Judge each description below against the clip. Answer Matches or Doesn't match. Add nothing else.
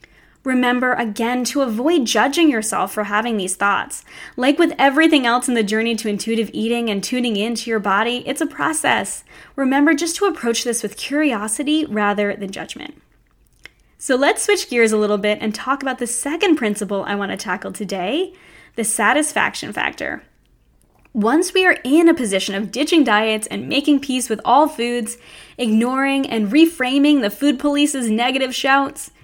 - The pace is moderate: Matches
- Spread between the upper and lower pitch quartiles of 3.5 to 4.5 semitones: Doesn't match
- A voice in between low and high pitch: Doesn't match